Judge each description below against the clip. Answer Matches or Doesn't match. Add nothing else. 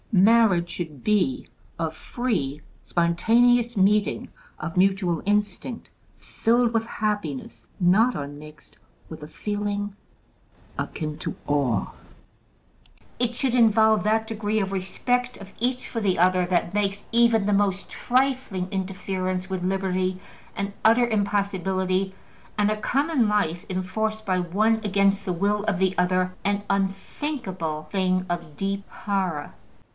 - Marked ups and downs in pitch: Doesn't match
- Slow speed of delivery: Matches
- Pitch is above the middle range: Matches